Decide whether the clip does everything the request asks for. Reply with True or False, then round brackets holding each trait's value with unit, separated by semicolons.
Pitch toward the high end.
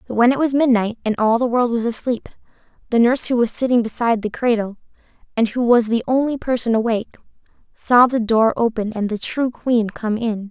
True (235 Hz)